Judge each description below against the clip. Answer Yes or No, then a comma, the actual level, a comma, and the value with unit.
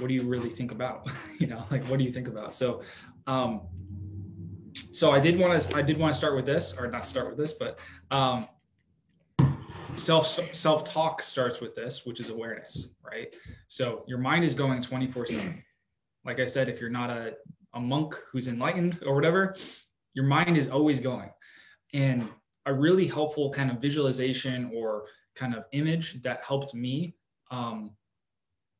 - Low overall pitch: Yes, low, 130 Hz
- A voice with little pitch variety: No, average, 3.9 semitones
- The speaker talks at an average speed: Yes, average, 175 wpm